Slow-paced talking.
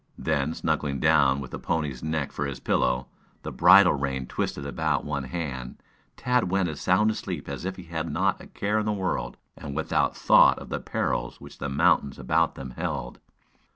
No: average, 190 wpm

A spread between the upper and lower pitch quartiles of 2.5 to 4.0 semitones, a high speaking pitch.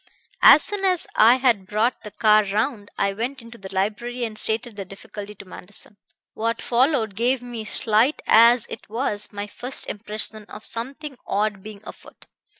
Yes: average, 2.8 semitones; high, 220 Hz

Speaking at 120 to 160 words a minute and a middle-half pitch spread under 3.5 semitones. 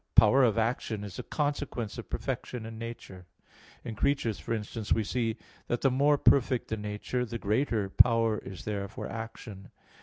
No: average, 175 wpm; average, 2.9 semitones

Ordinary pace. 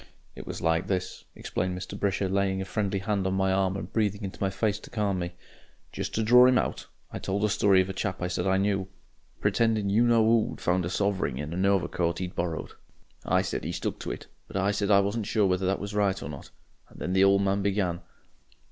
No: fast, 235 wpm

